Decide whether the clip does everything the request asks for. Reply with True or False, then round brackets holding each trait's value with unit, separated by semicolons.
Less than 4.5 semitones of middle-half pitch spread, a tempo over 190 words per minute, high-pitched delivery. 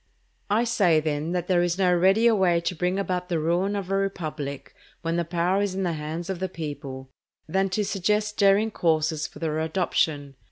False (3.5 semitones; 200 wpm; 175 Hz)